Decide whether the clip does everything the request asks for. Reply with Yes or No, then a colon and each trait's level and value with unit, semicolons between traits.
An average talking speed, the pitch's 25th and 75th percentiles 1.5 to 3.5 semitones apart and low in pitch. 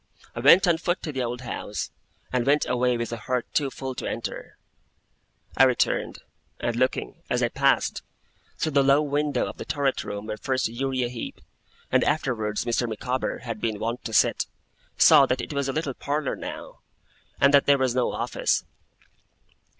Yes: average, 180 wpm; average, 3.0 semitones; low, 130 Hz